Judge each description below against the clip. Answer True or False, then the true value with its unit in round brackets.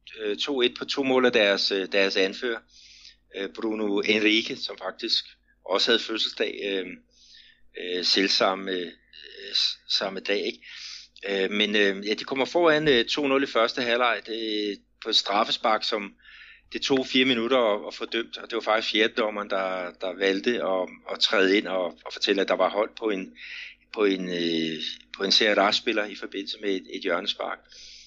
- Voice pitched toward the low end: True (105 Hz)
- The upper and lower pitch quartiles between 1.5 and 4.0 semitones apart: False (4.4 semitones)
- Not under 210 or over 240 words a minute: False (155 wpm)